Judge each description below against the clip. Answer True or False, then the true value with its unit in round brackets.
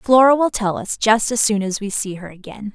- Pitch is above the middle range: True (215 Hz)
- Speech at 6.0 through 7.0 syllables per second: False (5.2 syllables/s)